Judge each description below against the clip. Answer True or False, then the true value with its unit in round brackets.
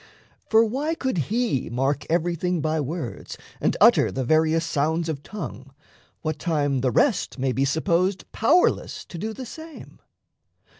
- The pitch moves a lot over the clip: True (7.1 semitones)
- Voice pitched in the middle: True (165 Hz)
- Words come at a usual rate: True (150 wpm)